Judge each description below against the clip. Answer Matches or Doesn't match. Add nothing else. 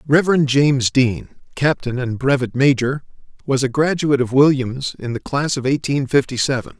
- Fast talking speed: Doesn't match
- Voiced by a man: Matches